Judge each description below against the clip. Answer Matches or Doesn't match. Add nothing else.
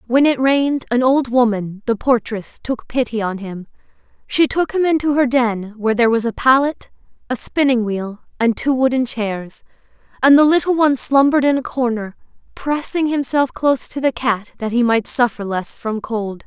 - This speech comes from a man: Doesn't match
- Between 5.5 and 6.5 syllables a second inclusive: Doesn't match